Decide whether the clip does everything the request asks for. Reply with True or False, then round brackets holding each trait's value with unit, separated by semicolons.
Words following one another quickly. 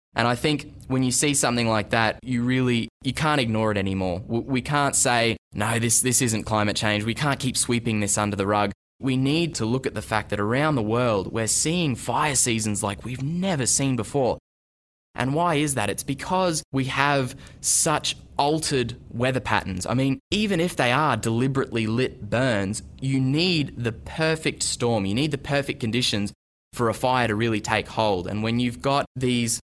False (195 wpm)